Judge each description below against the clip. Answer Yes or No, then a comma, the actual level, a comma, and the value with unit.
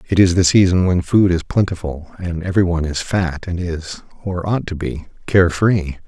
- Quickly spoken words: Yes, fast, 210 wpm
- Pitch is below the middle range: Yes, very low, 90 Hz